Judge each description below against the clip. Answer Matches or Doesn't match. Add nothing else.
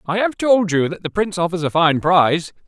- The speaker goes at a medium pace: Doesn't match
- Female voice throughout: Doesn't match